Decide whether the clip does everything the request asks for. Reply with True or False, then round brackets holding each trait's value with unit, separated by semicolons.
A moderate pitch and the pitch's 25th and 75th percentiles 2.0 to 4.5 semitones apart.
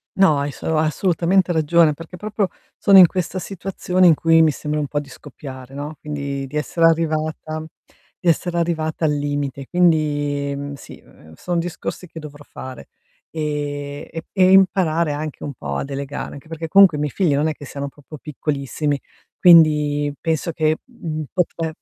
True (155 Hz; 2.7 semitones)